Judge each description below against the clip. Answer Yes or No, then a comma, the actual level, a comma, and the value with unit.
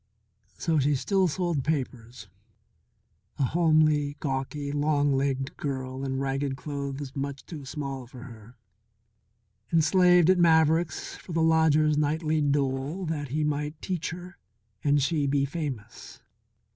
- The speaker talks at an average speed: No, slow, 130 wpm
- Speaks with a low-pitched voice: No, medium, 145 Hz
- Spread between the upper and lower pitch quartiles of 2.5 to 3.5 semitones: Yes, average, 2.9 semitones